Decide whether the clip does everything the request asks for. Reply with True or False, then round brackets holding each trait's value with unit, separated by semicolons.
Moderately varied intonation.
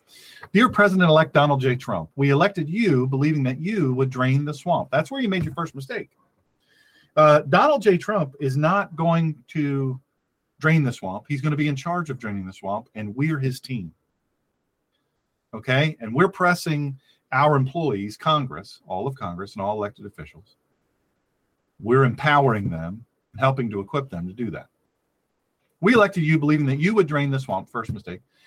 True (4.3 semitones)